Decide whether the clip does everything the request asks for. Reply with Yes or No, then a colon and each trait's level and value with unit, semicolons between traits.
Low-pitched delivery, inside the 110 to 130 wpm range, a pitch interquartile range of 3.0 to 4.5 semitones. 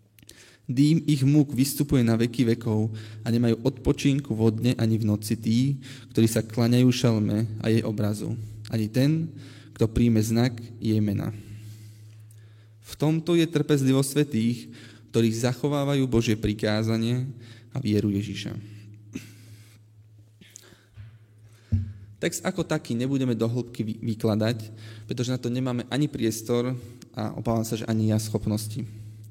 No: low, 115 Hz; average, 125 wpm; narrow, 2.6 semitones